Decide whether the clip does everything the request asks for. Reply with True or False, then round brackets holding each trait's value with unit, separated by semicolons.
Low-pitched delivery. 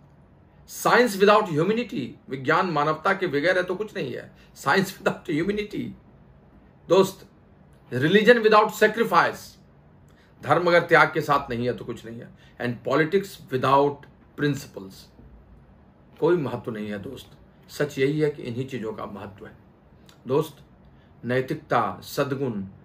False (145 Hz)